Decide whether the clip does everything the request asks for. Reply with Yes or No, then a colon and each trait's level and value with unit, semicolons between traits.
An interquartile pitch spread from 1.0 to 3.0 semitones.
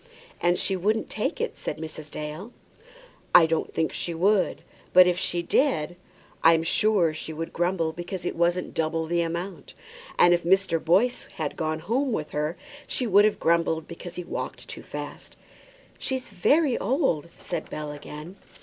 No: average, 3.4 semitones